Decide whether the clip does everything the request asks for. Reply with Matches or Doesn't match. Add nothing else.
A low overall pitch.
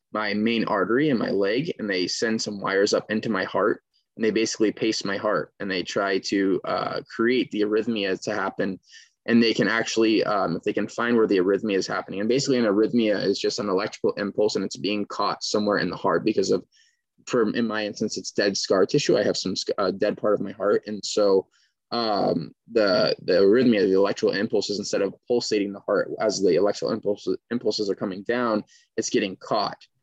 Matches